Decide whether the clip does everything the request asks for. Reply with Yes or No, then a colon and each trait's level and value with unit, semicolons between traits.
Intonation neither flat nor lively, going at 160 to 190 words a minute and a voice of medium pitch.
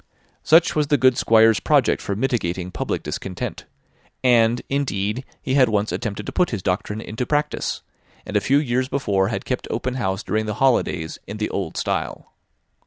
No: average, 4.5 semitones; average, 175 wpm; low, 115 Hz